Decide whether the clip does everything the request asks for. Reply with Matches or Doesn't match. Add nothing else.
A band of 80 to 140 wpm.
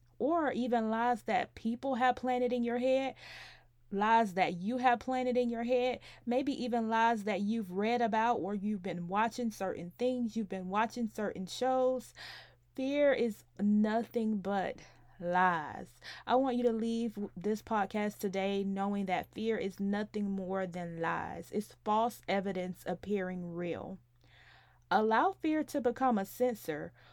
Doesn't match